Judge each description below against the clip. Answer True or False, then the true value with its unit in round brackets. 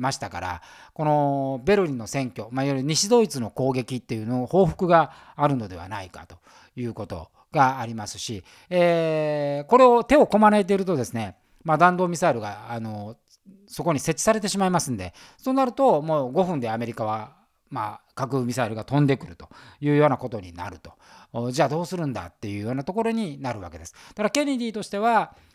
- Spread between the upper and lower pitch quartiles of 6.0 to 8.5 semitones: True (8.1 semitones)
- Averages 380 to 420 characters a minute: True (400 characters per minute)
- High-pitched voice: False (135 Hz)